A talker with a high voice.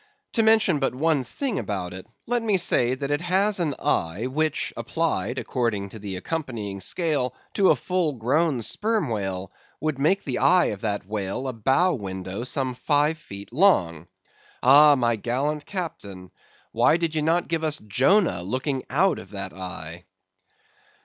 No: low, 130 Hz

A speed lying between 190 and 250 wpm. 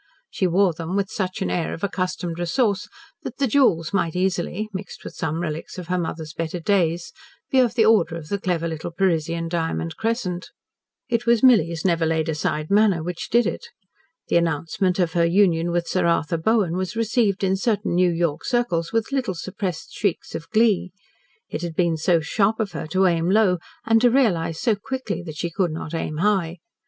Yes: average, 195 wpm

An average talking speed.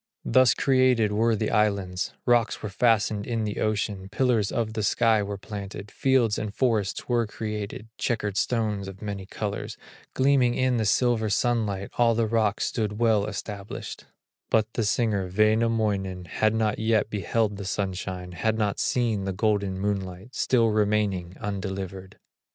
Yes: average, 150 wpm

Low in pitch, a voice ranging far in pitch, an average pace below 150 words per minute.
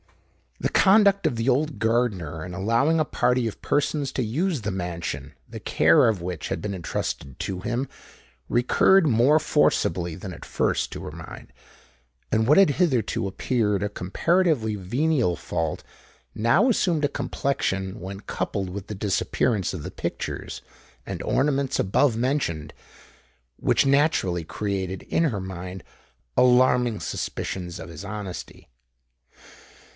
Yes: low, 110 Hz; wide, 6.8 semitones; average, 140 wpm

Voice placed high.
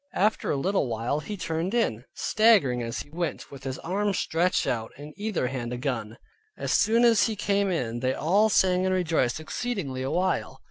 No: medium, 165 Hz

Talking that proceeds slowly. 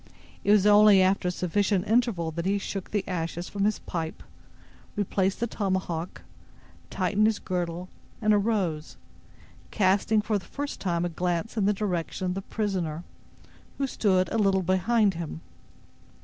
No: average, 155 wpm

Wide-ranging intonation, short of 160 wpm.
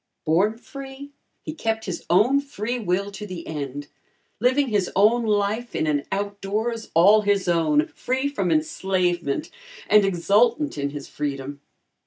Yes: wide, 5.8 semitones; average, 150 wpm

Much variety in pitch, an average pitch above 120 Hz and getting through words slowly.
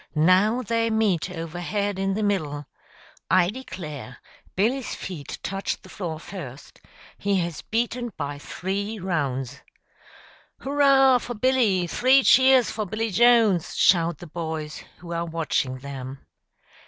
Yes: wide, 6.0 semitones; high, 190 Hz; slow, 130 wpm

